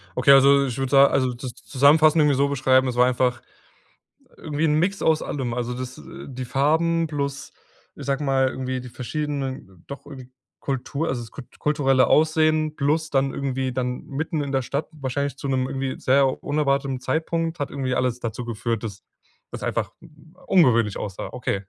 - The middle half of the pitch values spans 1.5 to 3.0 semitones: Yes, average, 2.7 semitones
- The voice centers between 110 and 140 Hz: Yes, low, 135 Hz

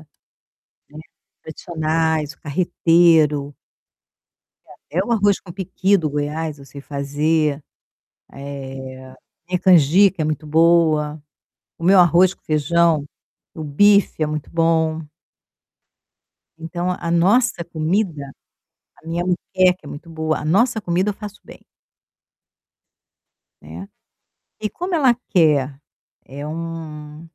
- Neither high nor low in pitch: Yes, medium, 165 Hz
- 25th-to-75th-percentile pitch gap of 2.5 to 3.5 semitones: Yes, average, 3.1 semitones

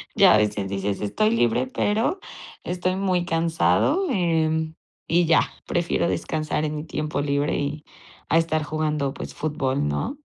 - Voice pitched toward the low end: No, medium, 155 Hz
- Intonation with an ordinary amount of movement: Yes, average, 3.5 semitones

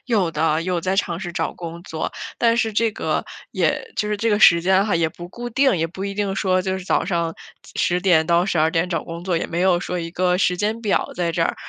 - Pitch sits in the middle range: Yes, medium, 180 Hz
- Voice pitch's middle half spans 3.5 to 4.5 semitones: No, average, 3.0 semitones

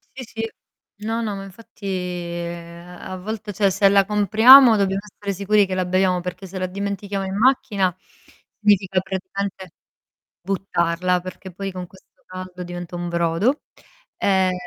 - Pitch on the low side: No, high, 190 Hz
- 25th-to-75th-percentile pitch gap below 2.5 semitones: Yes, narrow, 2.0 semitones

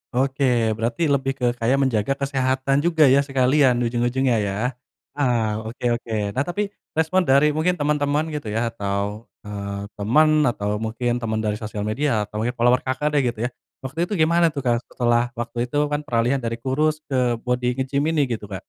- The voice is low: Yes, low, 125 Hz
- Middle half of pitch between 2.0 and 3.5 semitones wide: No, average, 4.0 semitones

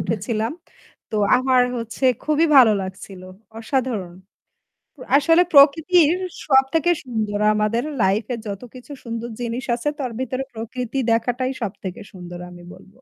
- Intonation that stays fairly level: No, average, 4.0 semitones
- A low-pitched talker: No, high, 240 Hz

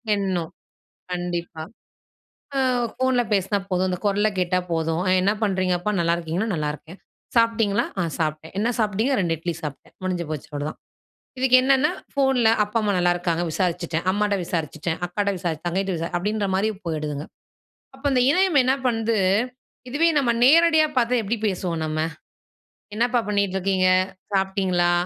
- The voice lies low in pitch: No, high, 190 Hz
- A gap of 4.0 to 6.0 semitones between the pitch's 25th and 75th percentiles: Yes, average, 4.8 semitones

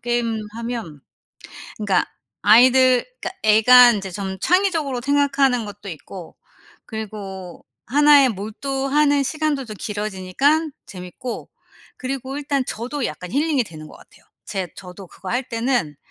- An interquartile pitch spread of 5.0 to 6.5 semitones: Yes, wide, 5.4 semitones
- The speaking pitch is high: Yes, high, 240 Hz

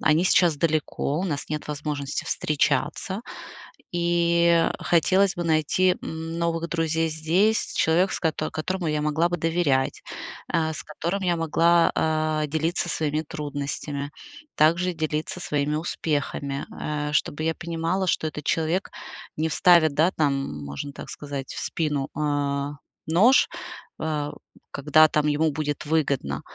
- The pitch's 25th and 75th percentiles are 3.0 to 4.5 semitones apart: No, narrow, 2.4 semitones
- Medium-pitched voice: Yes, medium, 155 Hz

